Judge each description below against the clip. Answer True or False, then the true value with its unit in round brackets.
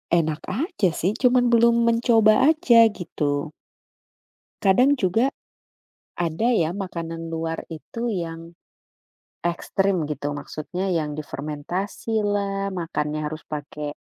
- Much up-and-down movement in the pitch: True (6.3 semitones)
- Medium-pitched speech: True (180 Hz)